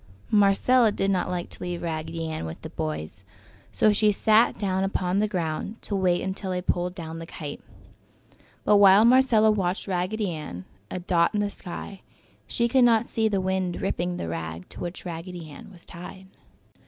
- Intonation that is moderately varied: Yes, average, 3.5 semitones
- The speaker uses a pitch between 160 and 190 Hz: Yes, medium, 185 Hz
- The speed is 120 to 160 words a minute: No, average, 180 wpm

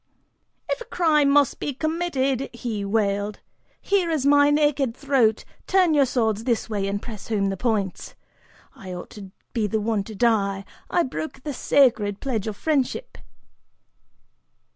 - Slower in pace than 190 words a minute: Yes, average, 155 wpm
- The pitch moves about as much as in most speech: No, wide, 5.7 semitones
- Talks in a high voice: Yes, high, 235 Hz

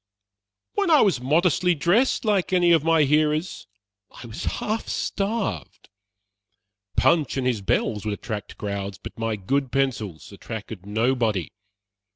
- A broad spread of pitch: Yes, wide, 8.3 semitones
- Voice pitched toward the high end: No, low, 135 Hz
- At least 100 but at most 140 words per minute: Yes, slow, 135 wpm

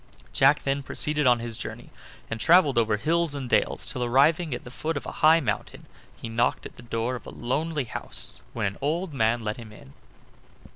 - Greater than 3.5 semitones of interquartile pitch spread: Yes, average, 4.7 semitones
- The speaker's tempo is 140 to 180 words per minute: No, fast, 205 wpm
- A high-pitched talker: No, low, 130 Hz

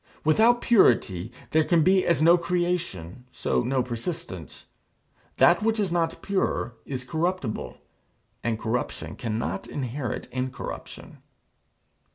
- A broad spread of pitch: Yes, wide, 7.0 semitones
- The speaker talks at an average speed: No, slow, 115 wpm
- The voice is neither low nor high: Yes, medium, 145 Hz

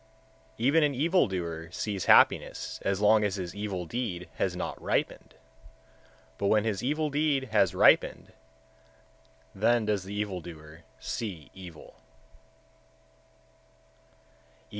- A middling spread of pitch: Yes, average, 4.9 semitones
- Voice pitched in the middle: No, low, 105 Hz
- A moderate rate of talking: No, slow, 120 wpm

